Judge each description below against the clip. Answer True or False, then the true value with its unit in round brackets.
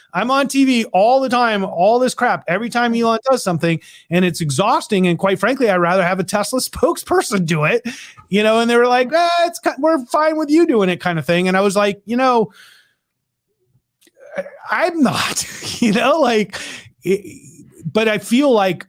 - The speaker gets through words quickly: False (195 wpm)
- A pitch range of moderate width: False (6.2 semitones)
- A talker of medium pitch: False (225 Hz)